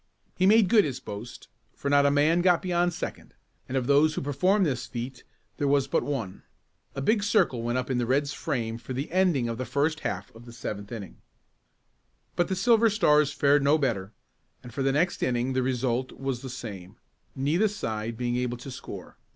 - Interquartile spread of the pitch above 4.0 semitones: Yes, average, 4.6 semitones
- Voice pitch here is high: No, low, 135 Hz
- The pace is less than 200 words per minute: No, fast, 205 wpm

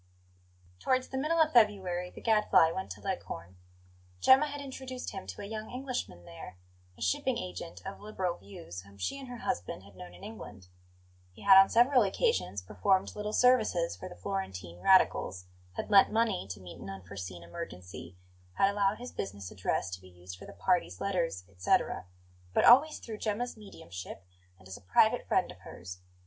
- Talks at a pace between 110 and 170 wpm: No, average, 180 wpm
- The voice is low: No, medium, 165 Hz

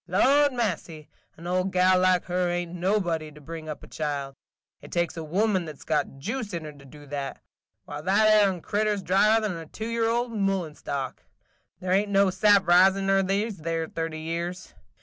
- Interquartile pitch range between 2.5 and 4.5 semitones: Yes, average, 3.9 semitones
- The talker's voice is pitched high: No, medium, 180 Hz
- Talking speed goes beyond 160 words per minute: Yes, fast, 205 wpm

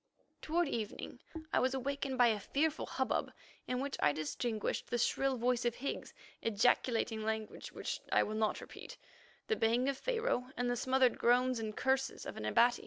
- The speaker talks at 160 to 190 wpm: Yes, average, 175 wpm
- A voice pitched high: Yes, high, 245 Hz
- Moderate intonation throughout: Yes, average, 3.0 semitones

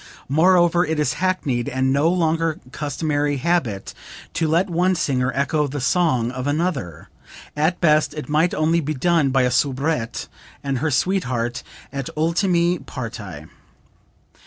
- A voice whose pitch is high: No, medium, 150 Hz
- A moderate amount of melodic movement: Yes, average, 4.4 semitones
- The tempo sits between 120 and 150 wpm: Yes, average, 140 wpm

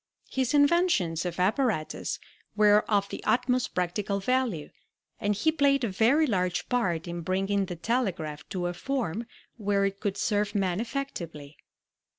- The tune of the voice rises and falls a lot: Yes, wide, 5.7 semitones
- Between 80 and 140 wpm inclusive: No, average, 150 wpm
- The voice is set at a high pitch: Yes, high, 205 Hz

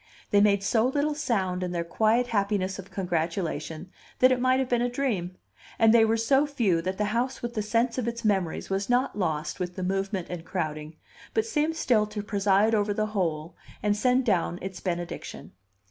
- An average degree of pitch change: Yes, average, 4.7 semitones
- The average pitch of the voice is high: Yes, high, 205 Hz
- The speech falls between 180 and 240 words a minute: Yes, average, 200 wpm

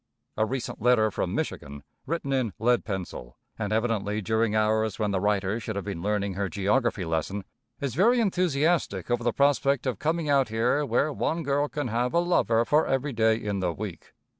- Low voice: Yes, low, 115 Hz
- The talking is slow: No, average, 190 wpm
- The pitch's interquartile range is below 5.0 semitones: No, average, 5.3 semitones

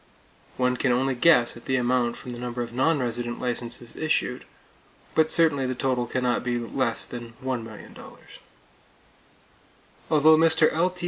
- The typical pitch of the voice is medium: No, low, 125 Hz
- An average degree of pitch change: Yes, average, 3.0 semitones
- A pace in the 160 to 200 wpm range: No, average, 150 wpm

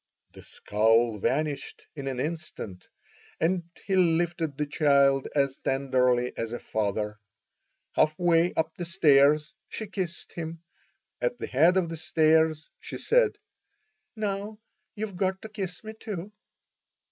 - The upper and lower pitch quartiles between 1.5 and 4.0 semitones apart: No, average, 4.8 semitones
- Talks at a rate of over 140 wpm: No, slow, 135 wpm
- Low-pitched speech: No, medium, 160 Hz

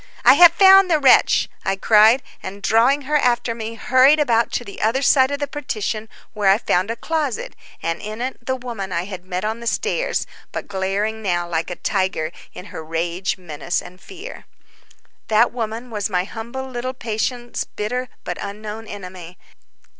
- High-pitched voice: Yes, high, 220 Hz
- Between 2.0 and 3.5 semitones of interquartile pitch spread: No, average, 4.9 semitones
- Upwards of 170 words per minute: Yes, average, 180 wpm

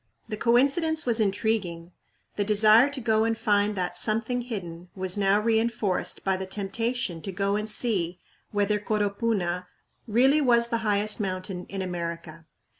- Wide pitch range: No, average, 3.5 semitones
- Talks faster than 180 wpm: No, average, 150 wpm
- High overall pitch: Yes, high, 210 Hz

